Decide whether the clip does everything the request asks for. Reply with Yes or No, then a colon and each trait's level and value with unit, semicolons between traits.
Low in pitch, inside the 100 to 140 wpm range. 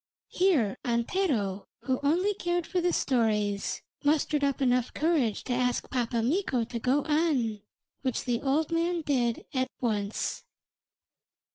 No: very high, 260 Hz; slow, 135 wpm